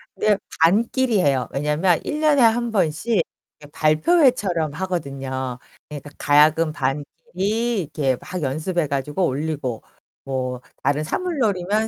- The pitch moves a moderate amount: No, wide, 6.6 semitones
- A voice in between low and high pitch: Yes, medium, 160 Hz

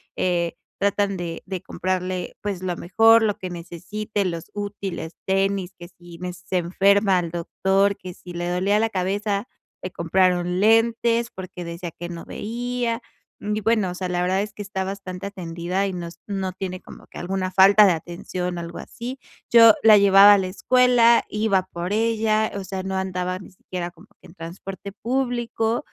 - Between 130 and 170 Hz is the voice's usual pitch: No, high, 190 Hz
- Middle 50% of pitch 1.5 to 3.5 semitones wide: Yes, average, 2.8 semitones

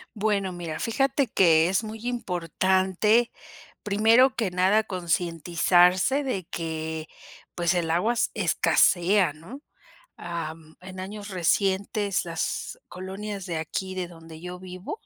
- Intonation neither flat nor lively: Yes, average, 3.4 semitones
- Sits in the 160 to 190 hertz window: Yes, medium, 185 Hz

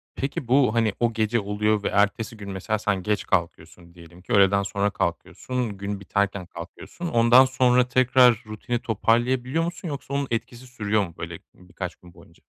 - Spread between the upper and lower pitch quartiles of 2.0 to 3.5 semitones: No, average, 3.9 semitones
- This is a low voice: Yes, low, 110 Hz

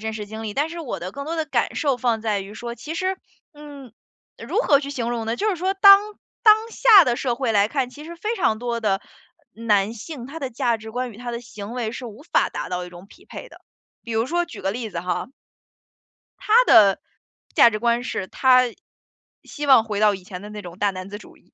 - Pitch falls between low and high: No, high, 235 Hz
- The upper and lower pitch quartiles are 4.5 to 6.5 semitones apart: Yes, average, 5.3 semitones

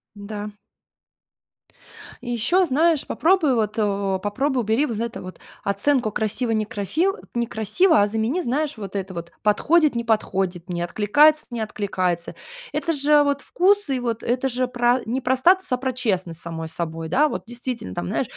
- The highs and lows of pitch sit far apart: Yes, wide, 5.7 semitones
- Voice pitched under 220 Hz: No, high, 235 Hz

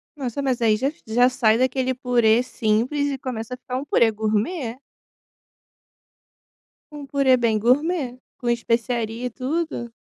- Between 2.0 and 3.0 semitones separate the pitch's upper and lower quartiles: Yes, average, 2.7 semitones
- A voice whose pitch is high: Yes, very high, 250 Hz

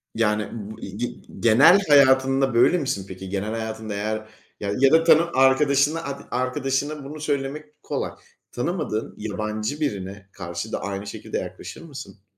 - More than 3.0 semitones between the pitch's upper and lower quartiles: Yes, average, 5.1 semitones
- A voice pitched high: No, low, 120 Hz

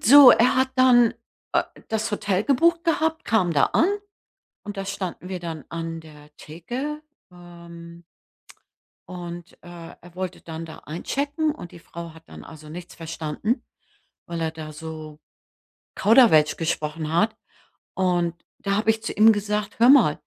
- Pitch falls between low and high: Yes, medium, 180 Hz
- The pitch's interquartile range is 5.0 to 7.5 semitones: Yes, wide, 5.4 semitones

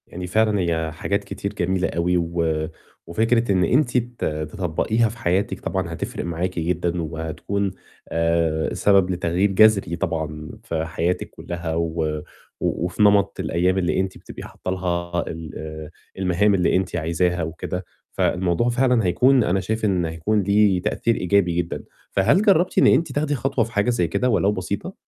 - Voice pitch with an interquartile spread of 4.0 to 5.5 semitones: No, average, 3.6 semitones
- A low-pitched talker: Yes, very low, 90 Hz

